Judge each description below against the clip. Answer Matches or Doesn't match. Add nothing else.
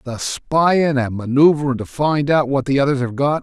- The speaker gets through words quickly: Matches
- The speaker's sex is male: Matches